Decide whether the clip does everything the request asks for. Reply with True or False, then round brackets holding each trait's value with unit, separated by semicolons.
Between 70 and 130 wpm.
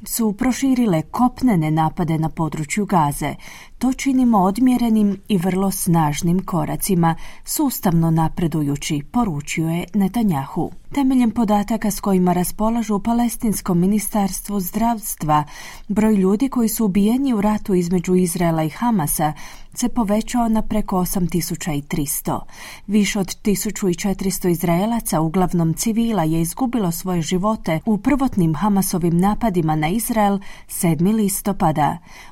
True (115 wpm)